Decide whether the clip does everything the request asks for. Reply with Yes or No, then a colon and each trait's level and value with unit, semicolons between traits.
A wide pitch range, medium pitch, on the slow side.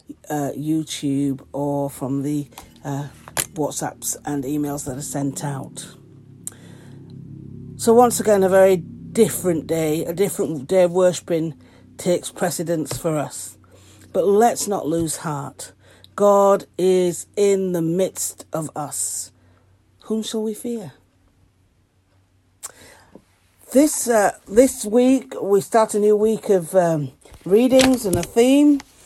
Yes: wide, 7.5 semitones; medium, 155 Hz; slow, 125 wpm